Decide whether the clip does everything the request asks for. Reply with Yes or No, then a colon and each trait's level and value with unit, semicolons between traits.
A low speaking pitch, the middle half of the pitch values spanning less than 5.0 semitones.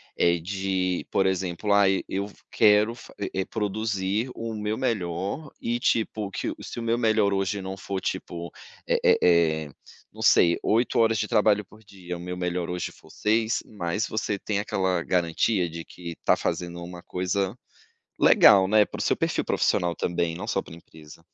Yes: very low, 95 Hz; average, 3.4 semitones